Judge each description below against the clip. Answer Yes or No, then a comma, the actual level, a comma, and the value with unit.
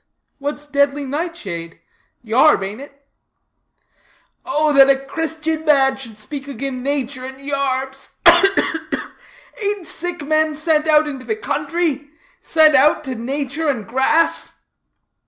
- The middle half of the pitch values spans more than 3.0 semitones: No, average, 2.7 semitones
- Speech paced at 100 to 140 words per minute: Yes, slow, 135 wpm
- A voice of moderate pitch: No, very high, 285 Hz